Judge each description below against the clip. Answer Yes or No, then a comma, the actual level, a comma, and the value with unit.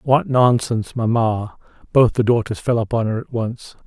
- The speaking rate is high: No, average, 170 wpm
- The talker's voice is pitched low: Yes, low, 115 Hz